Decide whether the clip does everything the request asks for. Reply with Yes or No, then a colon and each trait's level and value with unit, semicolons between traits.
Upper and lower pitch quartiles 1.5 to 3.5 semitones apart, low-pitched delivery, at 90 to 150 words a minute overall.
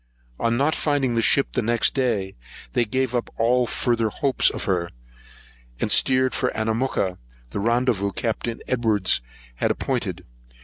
Yes: average, 2.8 semitones; low, 120 Hz; average, 140 wpm